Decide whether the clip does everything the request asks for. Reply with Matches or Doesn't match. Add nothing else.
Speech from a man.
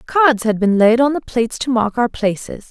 Doesn't match